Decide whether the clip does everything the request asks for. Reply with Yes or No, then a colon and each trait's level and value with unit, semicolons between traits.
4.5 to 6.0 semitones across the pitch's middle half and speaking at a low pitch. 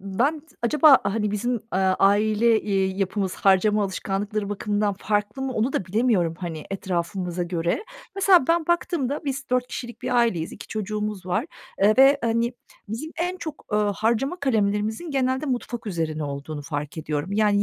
No: average, 4.8 semitones; high, 210 Hz